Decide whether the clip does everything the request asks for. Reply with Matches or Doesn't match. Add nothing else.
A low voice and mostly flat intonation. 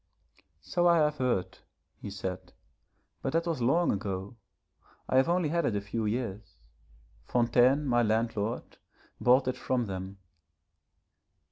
Doesn't match